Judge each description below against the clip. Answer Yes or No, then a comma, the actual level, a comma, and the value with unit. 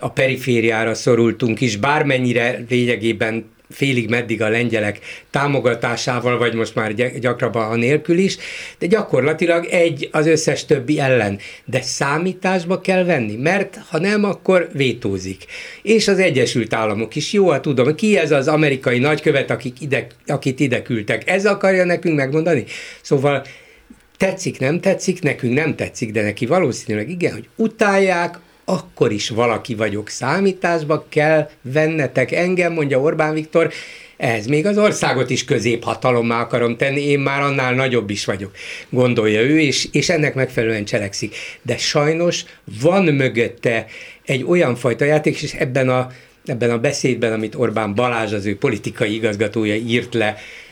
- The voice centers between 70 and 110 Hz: No, low, 135 Hz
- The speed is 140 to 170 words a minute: Yes, average, 145 wpm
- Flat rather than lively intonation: No, average, 5.3 semitones